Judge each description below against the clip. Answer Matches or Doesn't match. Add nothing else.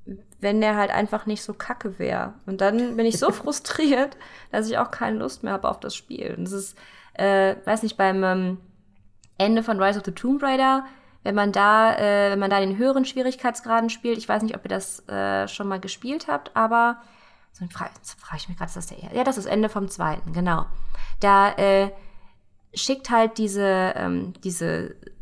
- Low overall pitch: Doesn't match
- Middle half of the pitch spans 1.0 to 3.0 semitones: Doesn't match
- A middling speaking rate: Doesn't match